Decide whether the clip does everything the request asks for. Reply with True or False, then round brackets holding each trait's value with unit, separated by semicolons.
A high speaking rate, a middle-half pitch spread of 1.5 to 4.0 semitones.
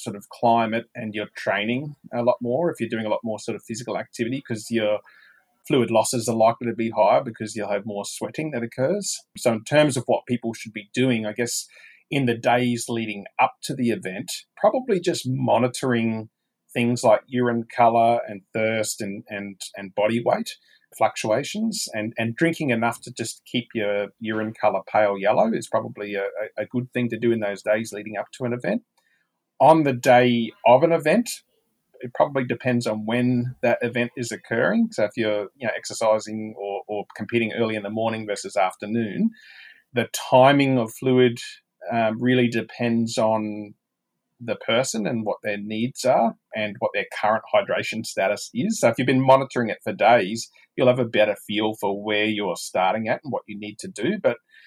False (190 wpm; 2.9 semitones)